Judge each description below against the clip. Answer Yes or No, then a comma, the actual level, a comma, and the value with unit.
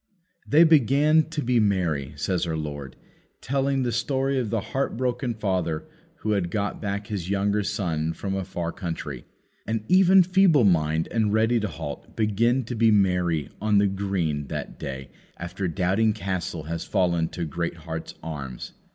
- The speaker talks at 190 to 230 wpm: No, average, 165 wpm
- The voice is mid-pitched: No, low, 100 Hz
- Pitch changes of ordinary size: No, wide, 5.9 semitones